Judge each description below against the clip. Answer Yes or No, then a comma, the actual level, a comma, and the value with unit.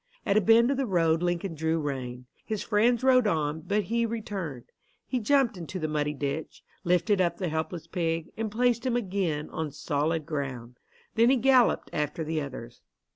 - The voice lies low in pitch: No, medium, 175 Hz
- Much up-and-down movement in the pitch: Yes, wide, 6.6 semitones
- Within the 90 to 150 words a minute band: No, average, 185 wpm